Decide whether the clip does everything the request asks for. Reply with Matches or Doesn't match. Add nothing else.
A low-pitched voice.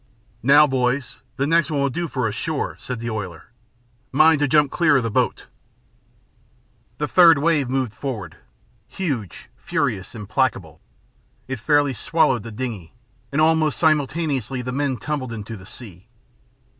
Matches